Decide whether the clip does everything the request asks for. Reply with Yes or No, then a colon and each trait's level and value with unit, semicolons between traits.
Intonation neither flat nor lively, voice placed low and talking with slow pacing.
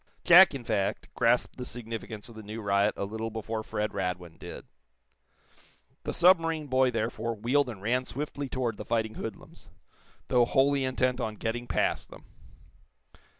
No: average, 3.1 semitones; low, 115 Hz; average, 155 wpm